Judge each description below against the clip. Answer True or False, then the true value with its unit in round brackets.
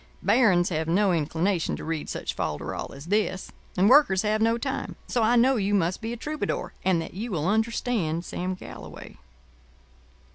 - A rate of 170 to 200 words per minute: True (175 wpm)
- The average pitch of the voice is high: True (195 Hz)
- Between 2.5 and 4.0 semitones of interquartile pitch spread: False (5.2 semitones)